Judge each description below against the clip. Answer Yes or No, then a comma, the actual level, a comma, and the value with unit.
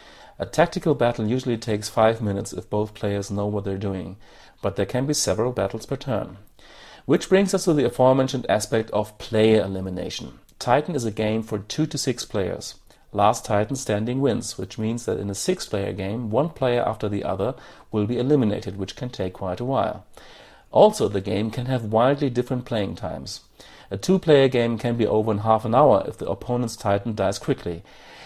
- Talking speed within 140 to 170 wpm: No, average, 195 wpm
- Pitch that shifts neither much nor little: Yes, average, 4.1 semitones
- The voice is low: Yes, low, 110 Hz